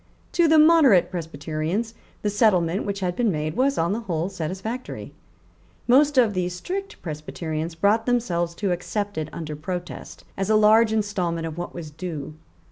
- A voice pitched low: No, medium, 185 Hz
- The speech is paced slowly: No, average, 165 wpm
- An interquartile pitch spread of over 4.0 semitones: Yes, average, 5.2 semitones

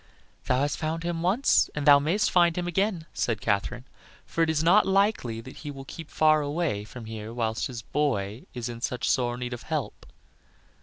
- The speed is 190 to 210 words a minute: Yes, average, 200 wpm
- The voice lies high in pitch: No, medium, 145 Hz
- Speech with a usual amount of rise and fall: No, wide, 5.8 semitones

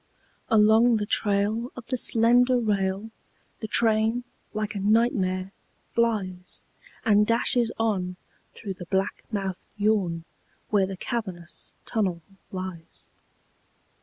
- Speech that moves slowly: Yes, slow, 110 wpm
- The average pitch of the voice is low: No, high, 210 Hz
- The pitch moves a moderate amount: Yes, average, 3.1 semitones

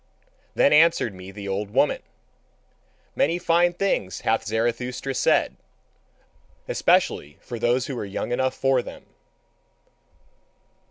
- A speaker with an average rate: No, slow, 115 wpm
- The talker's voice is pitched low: Yes, low, 120 Hz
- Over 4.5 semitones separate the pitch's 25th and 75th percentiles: Yes, average, 4.9 semitones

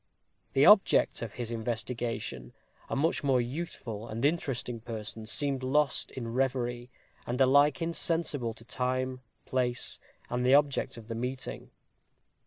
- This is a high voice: No, low, 125 Hz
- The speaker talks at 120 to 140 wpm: Yes, slow, 135 wpm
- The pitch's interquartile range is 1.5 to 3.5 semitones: Yes, average, 2.8 semitones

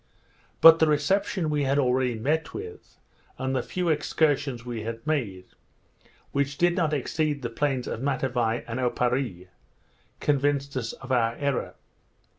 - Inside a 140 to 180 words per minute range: Yes, average, 145 wpm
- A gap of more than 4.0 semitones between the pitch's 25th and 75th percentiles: No, average, 3.7 semitones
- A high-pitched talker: No, low, 135 Hz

